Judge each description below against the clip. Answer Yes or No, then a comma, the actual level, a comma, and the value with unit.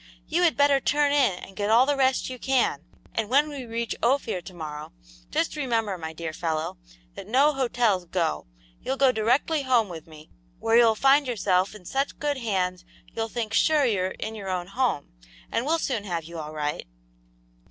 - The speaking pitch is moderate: No, high, 225 Hz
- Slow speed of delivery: No, average, 195 wpm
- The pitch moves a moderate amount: No, wide, 6.7 semitones